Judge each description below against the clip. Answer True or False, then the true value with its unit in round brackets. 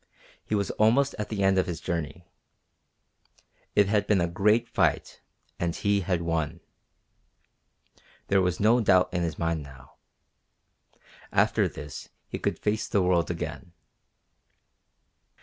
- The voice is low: True (90 Hz)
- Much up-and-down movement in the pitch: False (3.6 semitones)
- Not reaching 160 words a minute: True (135 wpm)